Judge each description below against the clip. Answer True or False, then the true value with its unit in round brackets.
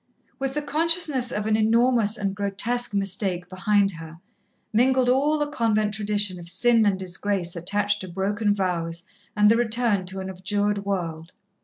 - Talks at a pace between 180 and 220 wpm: False (160 wpm)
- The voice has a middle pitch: False (205 Hz)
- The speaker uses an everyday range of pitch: True (3.8 semitones)